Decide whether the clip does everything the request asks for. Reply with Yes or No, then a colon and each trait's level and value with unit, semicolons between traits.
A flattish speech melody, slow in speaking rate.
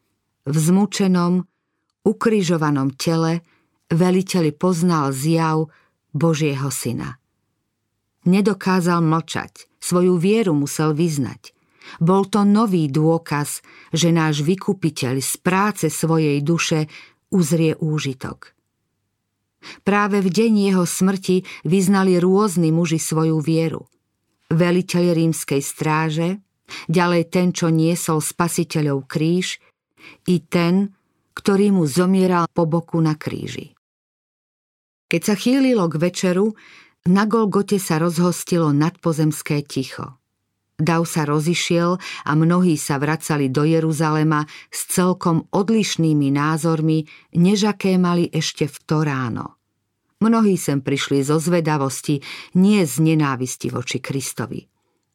No: average, 3.2 semitones; slow, 105 wpm